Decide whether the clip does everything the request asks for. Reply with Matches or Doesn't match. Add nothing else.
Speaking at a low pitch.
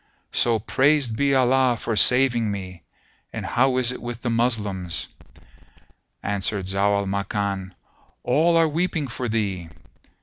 Matches